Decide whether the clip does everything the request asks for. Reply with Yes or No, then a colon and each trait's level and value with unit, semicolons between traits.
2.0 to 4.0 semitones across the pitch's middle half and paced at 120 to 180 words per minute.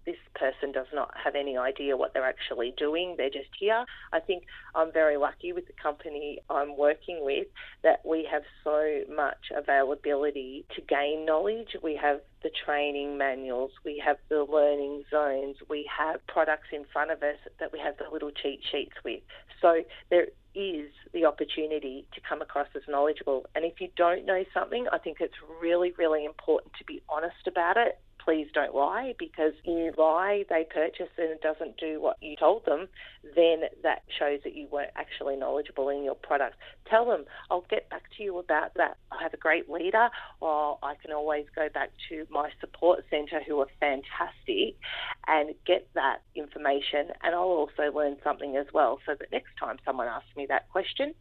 No: average, 2.8 semitones; average, 190 wpm